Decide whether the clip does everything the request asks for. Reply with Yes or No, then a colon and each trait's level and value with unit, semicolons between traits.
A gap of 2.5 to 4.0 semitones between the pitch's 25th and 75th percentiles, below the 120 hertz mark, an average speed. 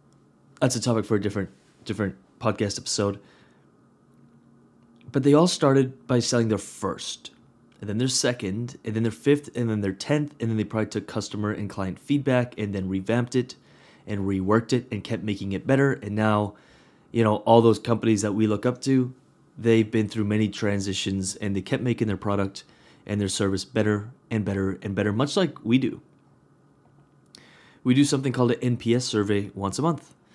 Yes: average, 3.4 semitones; low, 110 Hz; average, 190 wpm